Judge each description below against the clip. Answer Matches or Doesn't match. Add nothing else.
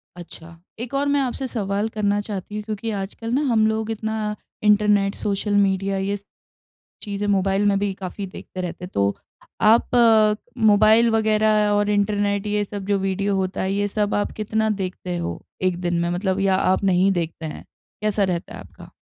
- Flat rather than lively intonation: Matches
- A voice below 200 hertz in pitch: Doesn't match